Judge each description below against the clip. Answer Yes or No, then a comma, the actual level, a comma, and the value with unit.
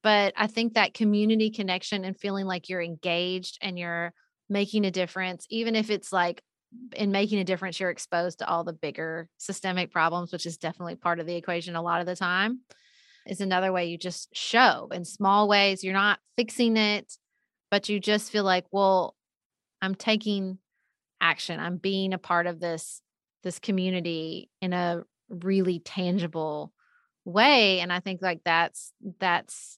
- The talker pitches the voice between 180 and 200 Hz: Yes, high, 190 Hz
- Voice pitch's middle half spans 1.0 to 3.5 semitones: Yes, average, 3.0 semitones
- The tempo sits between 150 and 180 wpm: Yes, average, 170 wpm